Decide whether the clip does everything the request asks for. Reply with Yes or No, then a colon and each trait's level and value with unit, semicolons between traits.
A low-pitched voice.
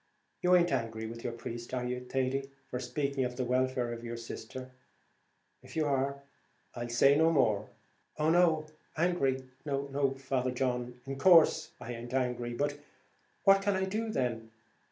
Yes: low, 130 Hz